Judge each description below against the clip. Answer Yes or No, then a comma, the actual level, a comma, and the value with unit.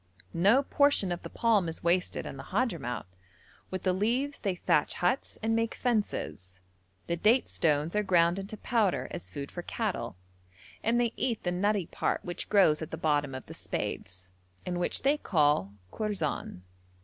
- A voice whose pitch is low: No, medium, 185 Hz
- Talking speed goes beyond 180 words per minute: No, average, 175 wpm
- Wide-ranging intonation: Yes, wide, 6.5 semitones